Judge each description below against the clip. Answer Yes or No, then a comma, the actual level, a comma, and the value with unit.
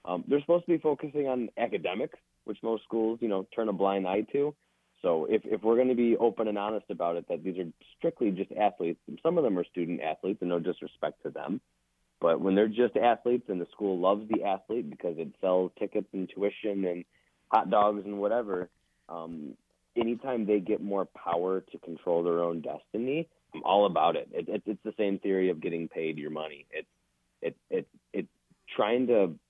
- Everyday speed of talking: No, fast, 210 wpm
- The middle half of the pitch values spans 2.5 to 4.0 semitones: No, average, 4.5 semitones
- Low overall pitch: Yes, low, 100 Hz